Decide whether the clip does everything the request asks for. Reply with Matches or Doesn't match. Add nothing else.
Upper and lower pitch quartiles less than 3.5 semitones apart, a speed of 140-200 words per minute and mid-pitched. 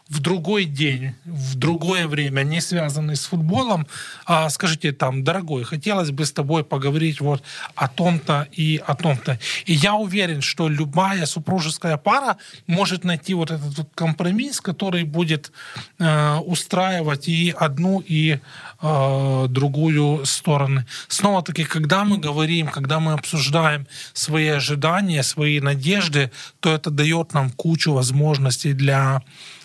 Doesn't match